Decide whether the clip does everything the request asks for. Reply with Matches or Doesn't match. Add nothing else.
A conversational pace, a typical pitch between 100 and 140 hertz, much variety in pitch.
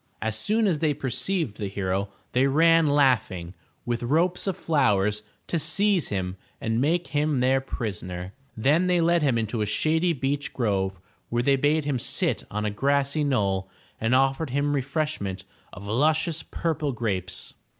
Matches